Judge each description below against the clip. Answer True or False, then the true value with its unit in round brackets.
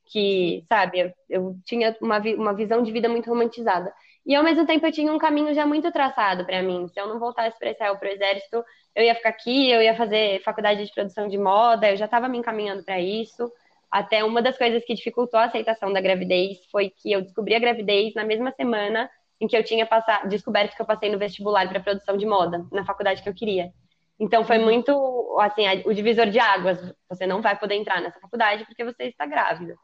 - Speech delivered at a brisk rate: True (225 wpm)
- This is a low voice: False (215 Hz)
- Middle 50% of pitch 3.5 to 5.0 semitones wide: False (2.9 semitones)